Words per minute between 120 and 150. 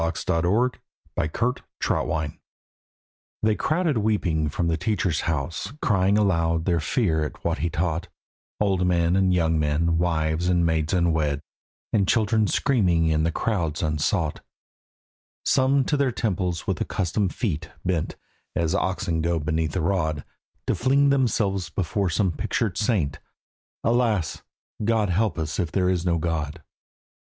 Yes: average, 140 wpm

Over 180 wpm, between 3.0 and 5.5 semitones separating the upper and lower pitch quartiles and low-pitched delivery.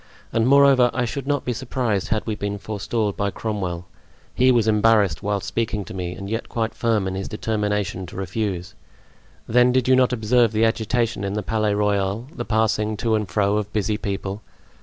No: average, 195 wpm; narrow, 2.5 semitones; low, 105 Hz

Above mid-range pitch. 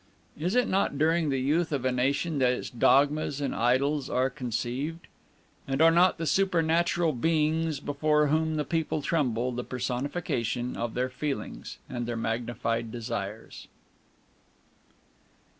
No: medium, 140 Hz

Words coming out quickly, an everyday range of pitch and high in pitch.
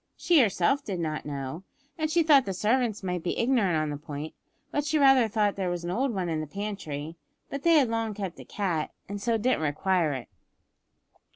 No: fast, 210 wpm; wide, 7.4 semitones; high, 200 Hz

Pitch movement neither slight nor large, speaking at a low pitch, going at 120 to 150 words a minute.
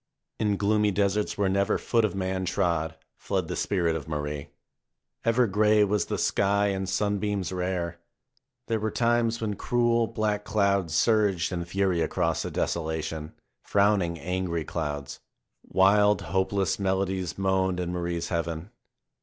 Yes: average, 3.3 semitones; very low, 95 Hz; average, 140 wpm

